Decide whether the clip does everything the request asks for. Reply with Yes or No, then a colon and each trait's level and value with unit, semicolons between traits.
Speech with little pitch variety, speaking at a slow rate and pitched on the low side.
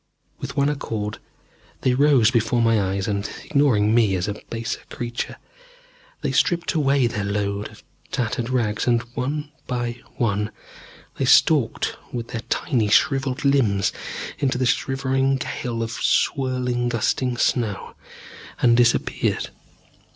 No: average, 3.4 semitones; slow, 130 wpm; low, 120 Hz